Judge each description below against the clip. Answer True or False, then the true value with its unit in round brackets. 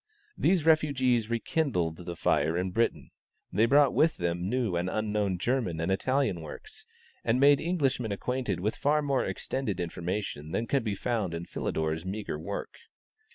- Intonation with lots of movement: True (7.0 semitones)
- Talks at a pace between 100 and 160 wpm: True (155 wpm)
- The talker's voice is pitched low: True (110 Hz)